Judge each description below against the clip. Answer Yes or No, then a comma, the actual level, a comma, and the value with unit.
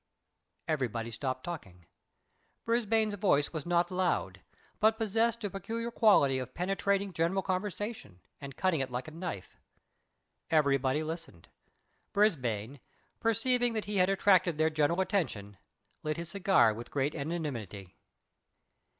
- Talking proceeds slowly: Yes, slow, 125 wpm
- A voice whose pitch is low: No, medium, 170 Hz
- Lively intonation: Yes, wide, 6.9 semitones